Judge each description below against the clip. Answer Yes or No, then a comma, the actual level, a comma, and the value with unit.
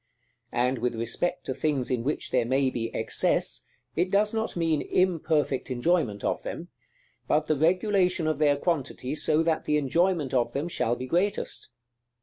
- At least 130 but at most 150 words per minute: No, average, 165 wpm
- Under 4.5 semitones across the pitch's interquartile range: No, average, 5.3 semitones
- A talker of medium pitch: Yes, medium, 150 Hz